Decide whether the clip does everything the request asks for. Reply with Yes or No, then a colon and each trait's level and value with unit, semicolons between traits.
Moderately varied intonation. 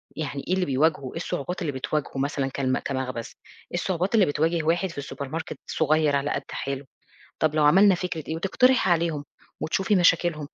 Yes: average, 3.8 semitones